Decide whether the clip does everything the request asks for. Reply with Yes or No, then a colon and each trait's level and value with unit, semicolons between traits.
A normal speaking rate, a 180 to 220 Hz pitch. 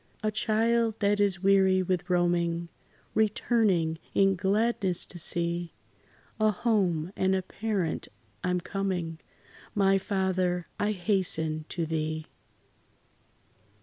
No: slow, 115 wpm; medium, 185 Hz